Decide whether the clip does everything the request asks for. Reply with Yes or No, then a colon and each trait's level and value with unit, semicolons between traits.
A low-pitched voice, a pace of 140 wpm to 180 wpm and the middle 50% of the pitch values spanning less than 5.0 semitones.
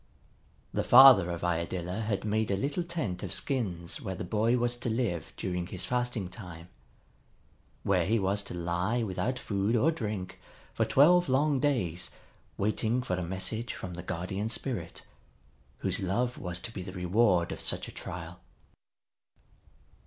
No: low, 100 Hz; average, 160 wpm; average, 5.3 semitones